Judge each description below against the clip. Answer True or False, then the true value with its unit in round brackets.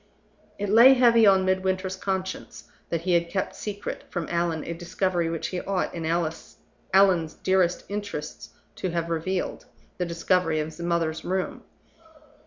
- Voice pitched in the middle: True (180 Hz)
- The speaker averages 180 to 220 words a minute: False (150 wpm)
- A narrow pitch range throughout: True (2.2 semitones)